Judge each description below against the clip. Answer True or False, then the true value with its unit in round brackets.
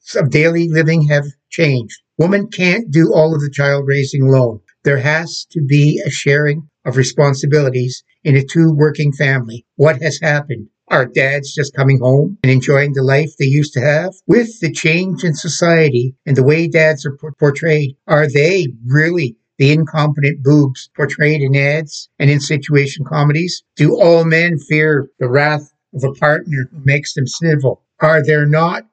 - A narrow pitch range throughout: True (2.2 semitones)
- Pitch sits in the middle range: True (150 Hz)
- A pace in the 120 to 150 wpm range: False (175 wpm)